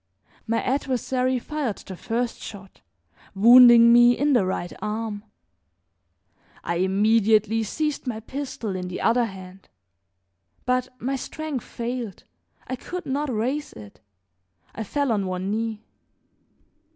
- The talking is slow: Yes, slow, 125 wpm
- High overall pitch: Yes, high, 230 Hz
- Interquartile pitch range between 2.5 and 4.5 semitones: Yes, average, 3.9 semitones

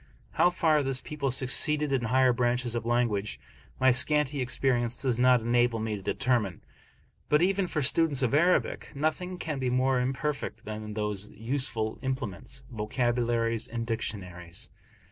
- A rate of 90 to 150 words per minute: Yes, average, 145 wpm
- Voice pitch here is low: Yes, low, 125 Hz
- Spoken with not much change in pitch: No, average, 3.3 semitones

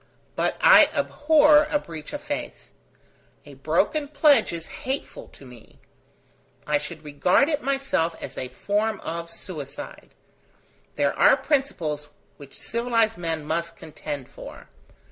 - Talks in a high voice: No, medium, 180 Hz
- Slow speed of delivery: Yes, slow, 130 wpm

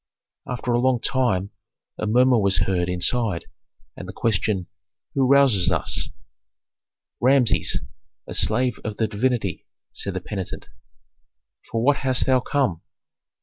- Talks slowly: Yes, slow, 130 wpm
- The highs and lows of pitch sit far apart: No, average, 4.7 semitones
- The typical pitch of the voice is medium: No, low, 115 Hz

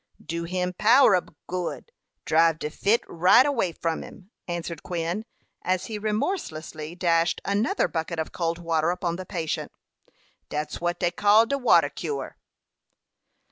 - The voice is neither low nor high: Yes, medium, 175 Hz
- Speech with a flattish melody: No, average, 3.8 semitones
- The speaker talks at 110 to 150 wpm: Yes, average, 145 wpm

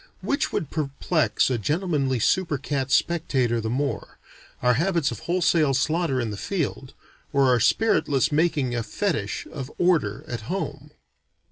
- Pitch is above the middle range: No, medium, 140 Hz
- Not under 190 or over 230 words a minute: No, average, 145 wpm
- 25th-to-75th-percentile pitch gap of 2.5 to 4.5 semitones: No, average, 5.1 semitones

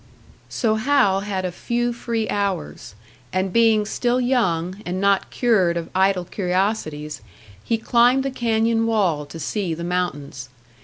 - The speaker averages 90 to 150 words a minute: Yes, average, 145 wpm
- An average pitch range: Yes, average, 4.4 semitones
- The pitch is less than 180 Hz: No, high, 200 Hz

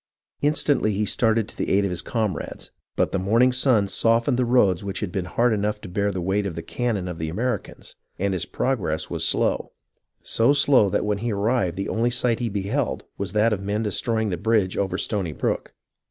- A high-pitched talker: No, low, 105 Hz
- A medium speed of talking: No, fast, 220 wpm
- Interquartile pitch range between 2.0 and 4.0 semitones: Yes, average, 3.4 semitones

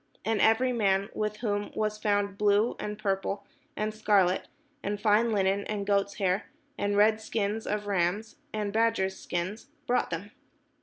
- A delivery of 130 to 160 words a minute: Yes, average, 155 wpm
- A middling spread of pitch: No, narrow, 1.5 semitones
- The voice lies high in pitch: Yes, high, 205 Hz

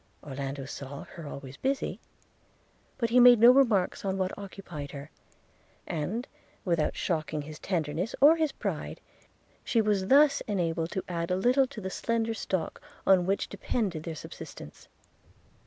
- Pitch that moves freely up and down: Yes, wide, 6.8 semitones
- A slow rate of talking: No, average, 155 wpm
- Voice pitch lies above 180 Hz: Yes, high, 190 Hz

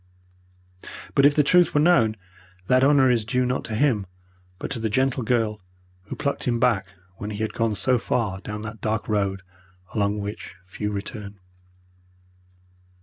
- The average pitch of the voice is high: No, low, 110 Hz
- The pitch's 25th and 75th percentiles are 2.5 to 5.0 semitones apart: Yes, average, 3.6 semitones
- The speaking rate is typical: Yes, average, 165 wpm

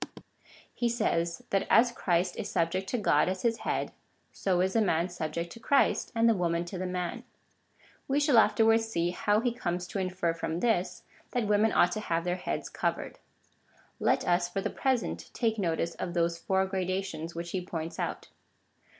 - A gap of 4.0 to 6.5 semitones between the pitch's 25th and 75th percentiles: Yes, average, 4.5 semitones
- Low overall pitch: No, medium, 185 Hz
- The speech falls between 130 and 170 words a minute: No, average, 185 wpm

